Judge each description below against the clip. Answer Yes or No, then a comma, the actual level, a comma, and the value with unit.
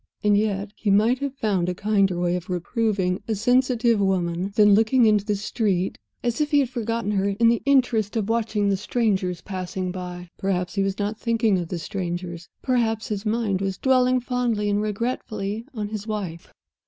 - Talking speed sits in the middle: Yes, average, 190 wpm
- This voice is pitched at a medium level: No, high, 210 Hz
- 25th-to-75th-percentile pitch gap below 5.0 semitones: Yes, average, 3.3 semitones